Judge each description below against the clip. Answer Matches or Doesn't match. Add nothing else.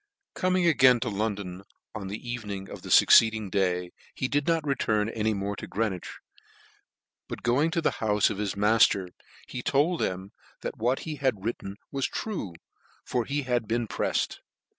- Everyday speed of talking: Matches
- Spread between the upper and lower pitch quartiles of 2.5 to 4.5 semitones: Doesn't match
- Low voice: Matches